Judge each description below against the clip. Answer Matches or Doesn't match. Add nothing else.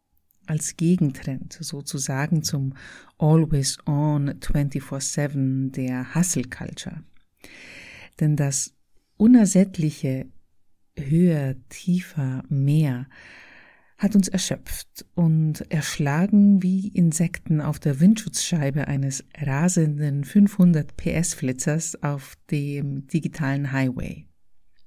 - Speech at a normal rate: Doesn't match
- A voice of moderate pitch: Matches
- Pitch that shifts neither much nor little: Matches